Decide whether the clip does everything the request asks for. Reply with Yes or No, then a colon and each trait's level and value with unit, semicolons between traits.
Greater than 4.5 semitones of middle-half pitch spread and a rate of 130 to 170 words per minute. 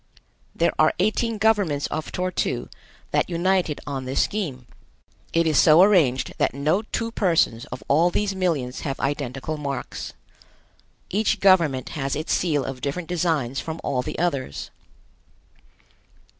Yes: average, 5.0 semitones; average, 145 wpm